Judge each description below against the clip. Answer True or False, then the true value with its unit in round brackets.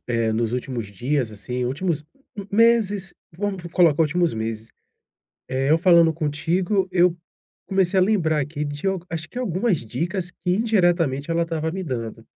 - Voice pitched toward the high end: False (165 Hz)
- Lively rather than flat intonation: True (5.7 semitones)